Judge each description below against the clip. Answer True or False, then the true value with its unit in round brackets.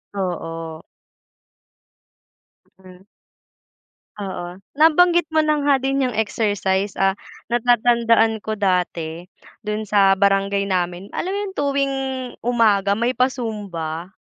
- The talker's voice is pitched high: True (210 Hz)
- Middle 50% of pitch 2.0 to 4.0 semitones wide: False (4.9 semitones)